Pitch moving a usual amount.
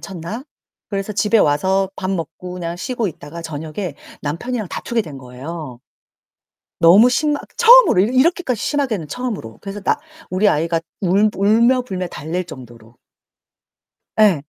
No: wide, 5.7 semitones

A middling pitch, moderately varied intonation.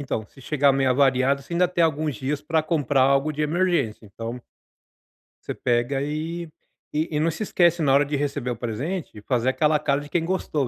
Yes: medium, 145 Hz; average, 3.3 semitones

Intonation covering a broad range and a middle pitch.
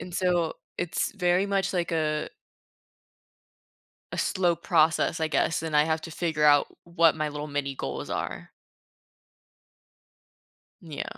No: narrow, 2.5 semitones; medium, 160 Hz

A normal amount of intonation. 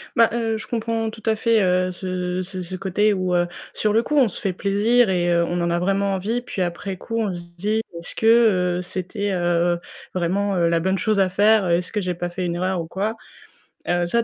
Yes: average, 3.5 semitones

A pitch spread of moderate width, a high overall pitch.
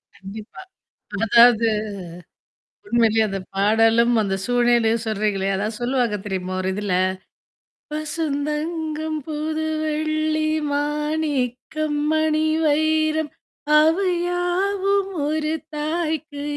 No: wide, 5.7 semitones; very high, 295 Hz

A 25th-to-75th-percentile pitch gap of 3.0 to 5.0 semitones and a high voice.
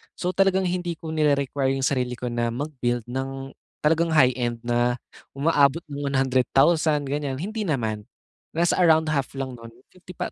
No: average, 4.1 semitones; medium, 140 Hz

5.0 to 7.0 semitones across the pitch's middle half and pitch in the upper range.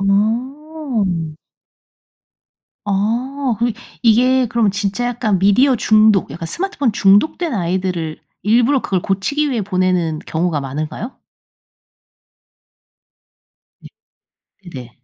Yes: wide, 5.4 semitones; high, 210 Hz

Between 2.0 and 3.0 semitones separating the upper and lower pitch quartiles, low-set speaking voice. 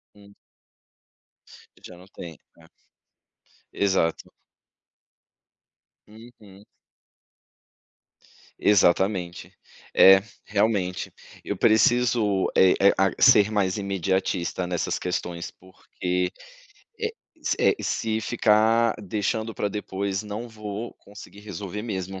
Yes: narrow, 2.6 semitones; low, 100 Hz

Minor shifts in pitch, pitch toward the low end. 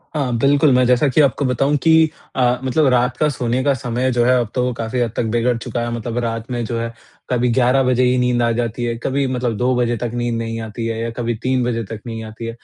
Yes: narrow, 1.6 semitones; low, 120 Hz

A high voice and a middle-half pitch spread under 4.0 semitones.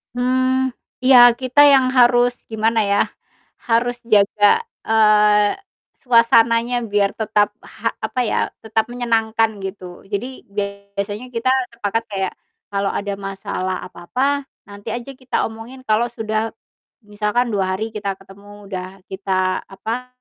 Yes: high, 220 Hz; average, 3.2 semitones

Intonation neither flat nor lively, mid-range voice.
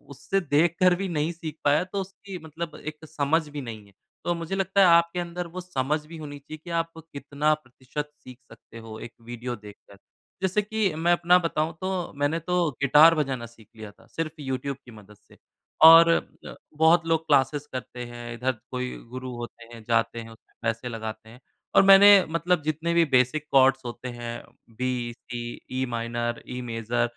No: wide, 5.8 semitones; medium, 145 Hz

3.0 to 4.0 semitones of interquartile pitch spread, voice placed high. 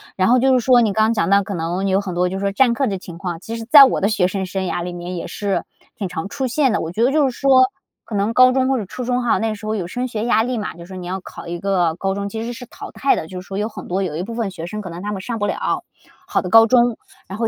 No: average, 4.4 semitones; high, 205 Hz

